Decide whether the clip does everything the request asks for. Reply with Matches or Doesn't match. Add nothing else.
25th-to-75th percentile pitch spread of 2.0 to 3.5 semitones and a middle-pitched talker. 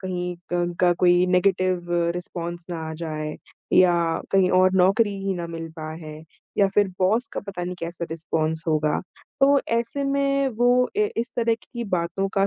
Matches